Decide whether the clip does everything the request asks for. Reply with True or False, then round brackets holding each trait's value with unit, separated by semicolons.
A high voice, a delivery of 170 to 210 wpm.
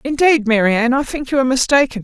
True (255 Hz; 205 wpm)